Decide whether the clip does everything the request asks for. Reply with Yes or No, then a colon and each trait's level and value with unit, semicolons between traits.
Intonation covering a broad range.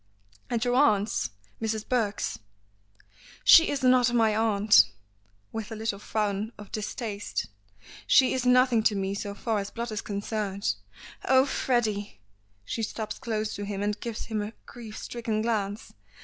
No: narrow, 2.4 semitones